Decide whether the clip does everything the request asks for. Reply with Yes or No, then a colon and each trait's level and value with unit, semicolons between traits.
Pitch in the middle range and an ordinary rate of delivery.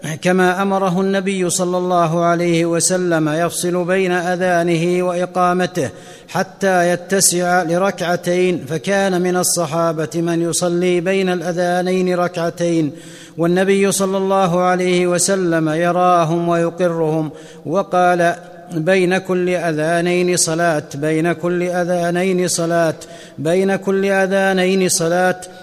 Yes: medium, 180 Hz; average, 110 wpm